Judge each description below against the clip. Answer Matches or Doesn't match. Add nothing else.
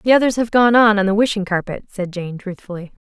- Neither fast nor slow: Doesn't match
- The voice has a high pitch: Matches